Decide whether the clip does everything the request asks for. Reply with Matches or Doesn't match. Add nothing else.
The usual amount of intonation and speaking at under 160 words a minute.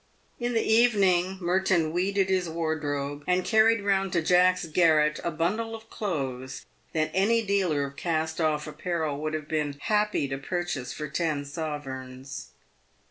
Matches